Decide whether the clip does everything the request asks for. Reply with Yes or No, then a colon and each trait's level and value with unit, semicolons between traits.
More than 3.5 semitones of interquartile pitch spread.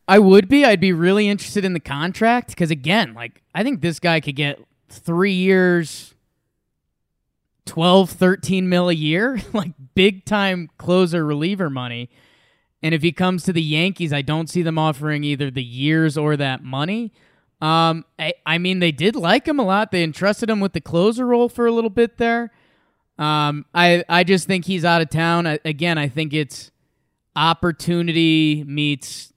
Yes: average, 4.1 semitones